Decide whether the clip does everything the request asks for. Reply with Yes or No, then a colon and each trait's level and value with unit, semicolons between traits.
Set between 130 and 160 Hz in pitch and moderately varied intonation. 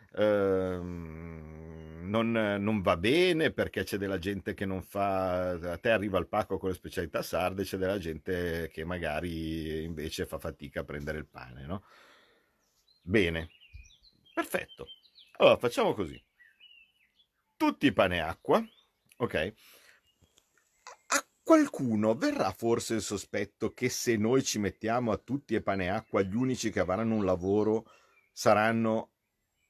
No: very low, 95 Hz; average, 4.6 semitones